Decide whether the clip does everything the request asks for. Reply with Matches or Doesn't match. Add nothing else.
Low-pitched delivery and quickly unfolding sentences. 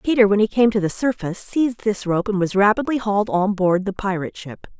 Doesn't match